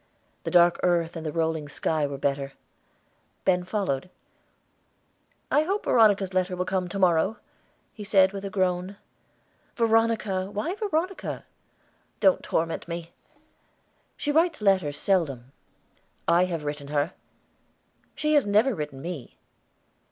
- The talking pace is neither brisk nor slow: No, slow, 130 wpm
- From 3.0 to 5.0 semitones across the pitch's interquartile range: Yes, average, 4.4 semitones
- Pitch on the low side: No, medium, 185 Hz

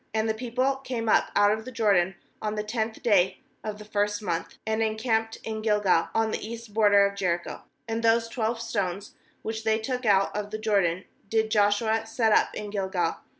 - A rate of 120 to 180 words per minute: No, average, 195 wpm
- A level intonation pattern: Yes, narrow, 1.6 semitones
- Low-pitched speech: No, high, 220 Hz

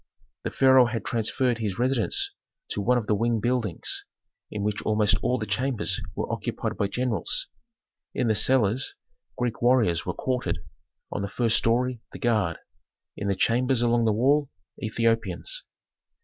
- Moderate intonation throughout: Yes, average, 3.0 semitones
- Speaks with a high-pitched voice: No, low, 115 Hz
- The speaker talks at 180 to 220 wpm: No, average, 155 wpm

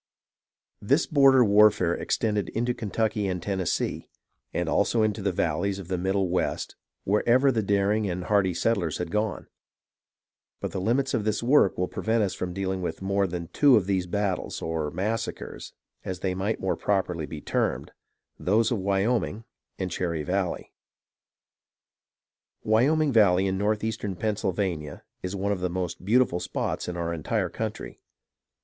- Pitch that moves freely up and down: No, average, 3.2 semitones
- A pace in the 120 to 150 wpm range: No, average, 165 wpm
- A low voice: Yes, low, 100 Hz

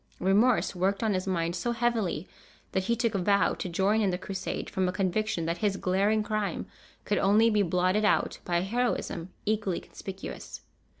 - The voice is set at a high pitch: Yes, high, 195 Hz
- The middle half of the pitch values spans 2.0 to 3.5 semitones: Yes, average, 2.8 semitones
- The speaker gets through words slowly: No, average, 185 wpm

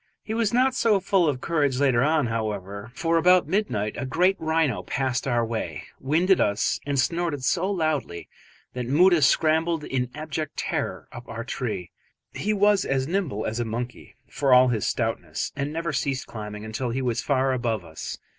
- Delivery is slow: No, average, 180 wpm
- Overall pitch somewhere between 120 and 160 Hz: Yes, low, 135 Hz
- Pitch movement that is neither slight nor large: No, wide, 5.9 semitones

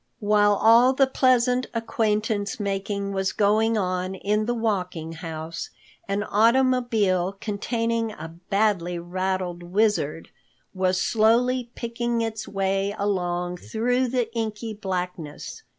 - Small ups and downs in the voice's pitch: No, average, 3.7 semitones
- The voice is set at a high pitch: Yes, high, 205 Hz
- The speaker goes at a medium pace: No, slow, 115 wpm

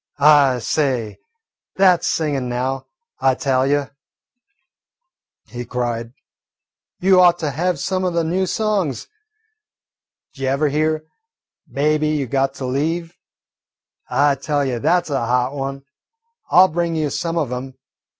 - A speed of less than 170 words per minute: Yes, average, 140 wpm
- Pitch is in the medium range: Yes, medium, 145 Hz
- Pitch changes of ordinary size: Yes, average, 4.0 semitones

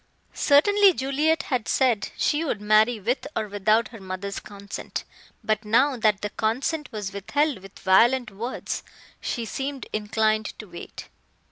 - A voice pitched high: Yes, high, 220 Hz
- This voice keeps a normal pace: Yes, average, 145 wpm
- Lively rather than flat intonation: No, average, 4.5 semitones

